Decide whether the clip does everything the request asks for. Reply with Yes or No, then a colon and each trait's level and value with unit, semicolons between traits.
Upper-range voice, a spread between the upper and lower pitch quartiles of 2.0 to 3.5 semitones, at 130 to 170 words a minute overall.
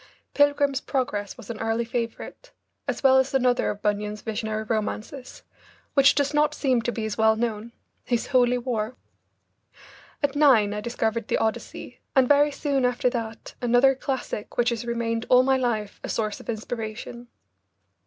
Yes: high, 240 Hz; average, 3.1 semitones; average, 165 wpm